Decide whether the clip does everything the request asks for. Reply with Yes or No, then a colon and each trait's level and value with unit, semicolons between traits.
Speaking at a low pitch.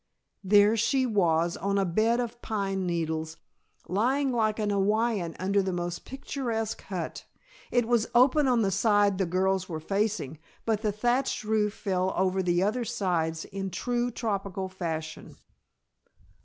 No: high, 200 Hz